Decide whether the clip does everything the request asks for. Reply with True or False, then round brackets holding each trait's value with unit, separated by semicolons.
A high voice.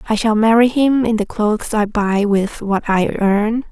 True (215 Hz)